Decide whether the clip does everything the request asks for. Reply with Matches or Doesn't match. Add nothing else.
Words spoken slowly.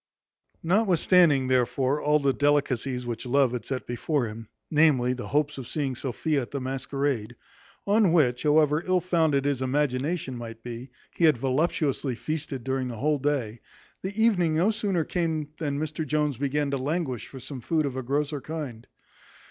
Doesn't match